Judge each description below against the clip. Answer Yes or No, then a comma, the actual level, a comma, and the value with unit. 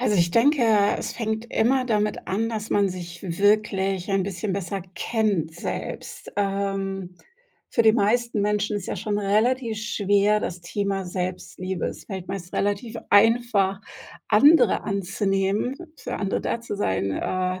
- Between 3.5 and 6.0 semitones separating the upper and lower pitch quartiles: No, narrow, 2.4 semitones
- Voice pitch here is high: Yes, high, 200 Hz